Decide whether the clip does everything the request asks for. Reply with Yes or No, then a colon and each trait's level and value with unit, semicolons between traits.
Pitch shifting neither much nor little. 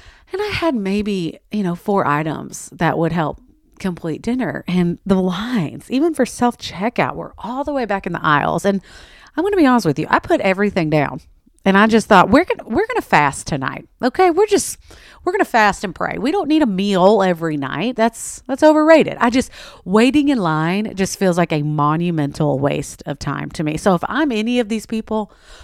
No: wide, 6.8 semitones